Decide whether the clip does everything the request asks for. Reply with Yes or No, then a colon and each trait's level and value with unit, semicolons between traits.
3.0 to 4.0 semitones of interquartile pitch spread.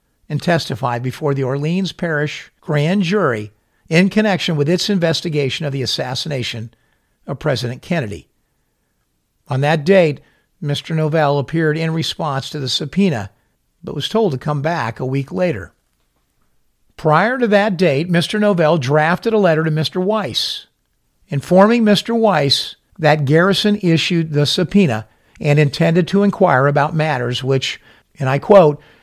No: average, 4.9 semitones